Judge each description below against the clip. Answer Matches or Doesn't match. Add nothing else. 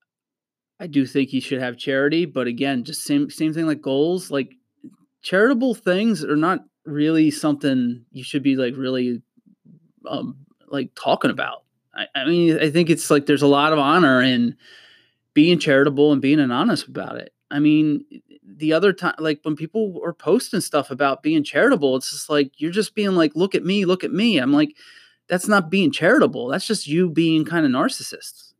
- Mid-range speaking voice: Matches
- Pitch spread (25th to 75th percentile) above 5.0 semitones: Matches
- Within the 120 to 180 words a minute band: Doesn't match